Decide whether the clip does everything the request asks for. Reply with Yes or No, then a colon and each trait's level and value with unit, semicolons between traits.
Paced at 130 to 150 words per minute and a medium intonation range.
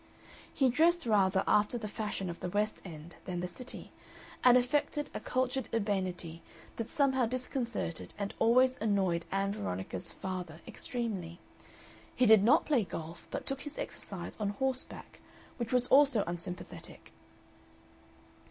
No: average, 140 wpm; wide, 5.9 semitones